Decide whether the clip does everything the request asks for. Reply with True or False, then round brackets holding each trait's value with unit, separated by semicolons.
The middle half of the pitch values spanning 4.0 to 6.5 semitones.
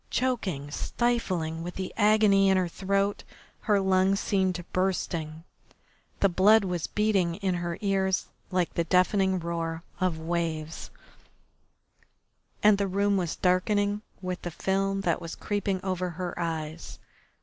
False (2.6 semitones)